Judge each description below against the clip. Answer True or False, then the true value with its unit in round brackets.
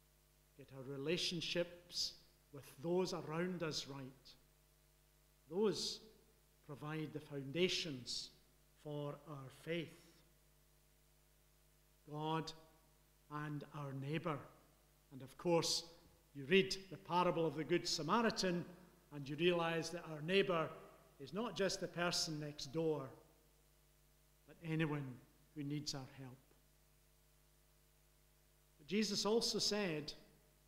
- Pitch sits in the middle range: True (155 Hz)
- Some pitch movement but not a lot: False (2.0 semitones)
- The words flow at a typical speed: False (105 wpm)